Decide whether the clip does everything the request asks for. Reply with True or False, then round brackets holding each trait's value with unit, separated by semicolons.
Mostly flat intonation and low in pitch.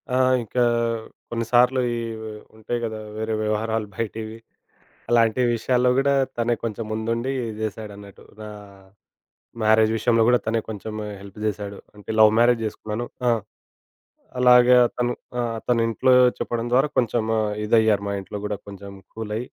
True (2.0 semitones; 110 Hz)